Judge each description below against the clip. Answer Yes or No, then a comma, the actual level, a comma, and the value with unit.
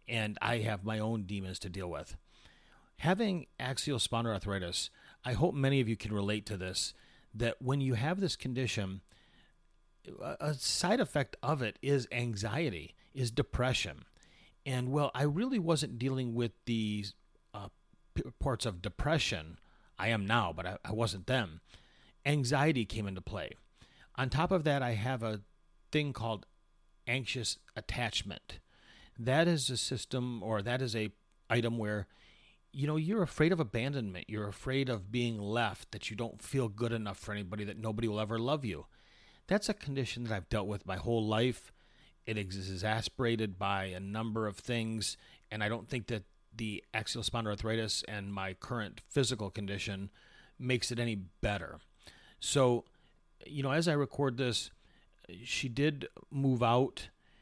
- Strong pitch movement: No, average, 4.2 semitones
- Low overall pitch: Yes, low, 115 Hz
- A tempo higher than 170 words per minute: No, average, 160 wpm